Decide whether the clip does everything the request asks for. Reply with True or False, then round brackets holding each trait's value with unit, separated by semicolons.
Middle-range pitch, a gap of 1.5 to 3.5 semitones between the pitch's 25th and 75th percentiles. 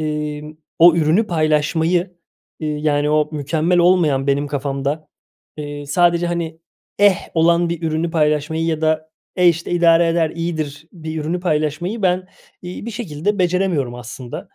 True (160 Hz; 2.5 semitones)